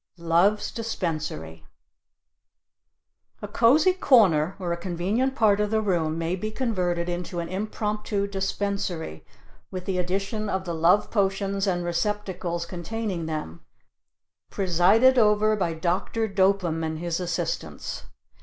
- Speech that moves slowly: Yes, slow, 125 wpm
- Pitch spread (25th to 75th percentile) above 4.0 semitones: No, average, 3.5 semitones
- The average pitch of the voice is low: No, high, 190 Hz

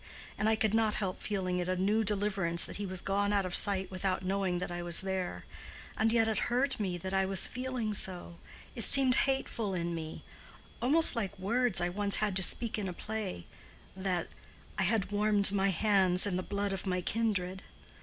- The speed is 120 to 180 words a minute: No, average, 195 wpm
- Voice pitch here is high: Yes, high, 195 Hz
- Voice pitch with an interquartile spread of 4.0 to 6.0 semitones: No, average, 2.8 semitones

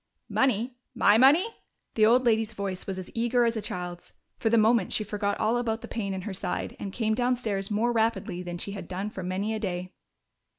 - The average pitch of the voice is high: Yes, high, 215 Hz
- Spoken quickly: Yes, fast, 215 wpm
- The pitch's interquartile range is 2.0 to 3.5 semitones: Yes, average, 3.2 semitones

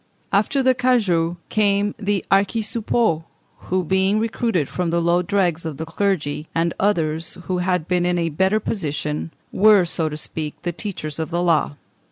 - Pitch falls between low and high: Yes, medium, 180 Hz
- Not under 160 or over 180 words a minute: Yes, average, 170 wpm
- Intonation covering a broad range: No, average, 3.8 semitones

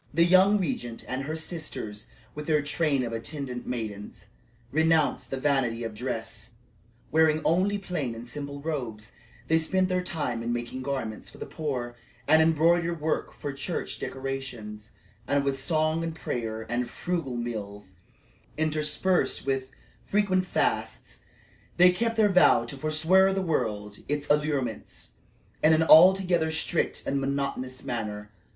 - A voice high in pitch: No, medium, 140 Hz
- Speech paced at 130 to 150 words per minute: Yes, average, 145 wpm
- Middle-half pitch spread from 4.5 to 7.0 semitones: Yes, average, 5.2 semitones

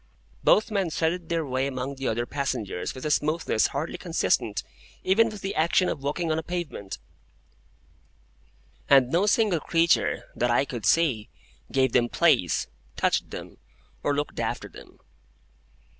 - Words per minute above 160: No, average, 150 wpm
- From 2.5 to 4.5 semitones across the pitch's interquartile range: No, average, 4.9 semitones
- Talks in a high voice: No, medium, 150 Hz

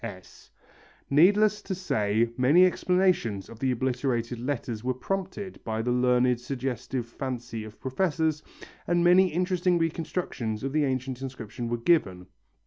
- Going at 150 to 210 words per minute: No, slow, 135 wpm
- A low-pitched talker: Yes, low, 130 Hz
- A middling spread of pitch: No, wide, 6.7 semitones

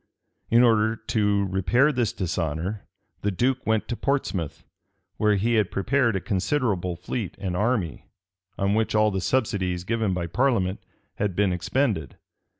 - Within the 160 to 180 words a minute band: No, average, 150 wpm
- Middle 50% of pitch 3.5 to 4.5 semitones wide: Yes, average, 4.2 semitones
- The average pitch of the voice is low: Yes, low, 105 Hz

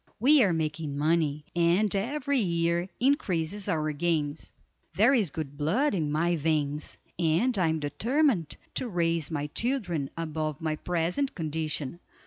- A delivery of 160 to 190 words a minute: No, average, 140 wpm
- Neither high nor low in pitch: Yes, medium, 165 Hz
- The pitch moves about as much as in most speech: Yes, average, 4.8 semitones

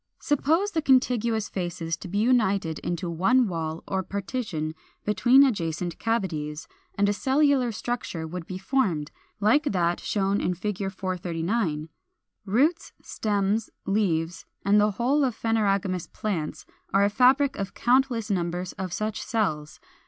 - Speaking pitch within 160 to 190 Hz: No, high, 200 Hz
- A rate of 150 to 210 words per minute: No, slow, 135 wpm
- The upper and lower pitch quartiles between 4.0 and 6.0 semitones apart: Yes, wide, 5.4 semitones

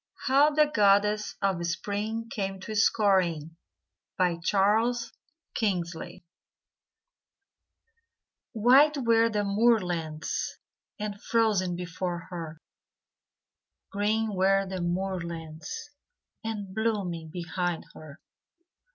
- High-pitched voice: Yes, high, 195 Hz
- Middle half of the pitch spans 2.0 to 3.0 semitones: No, average, 4.1 semitones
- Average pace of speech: No, slow, 80 wpm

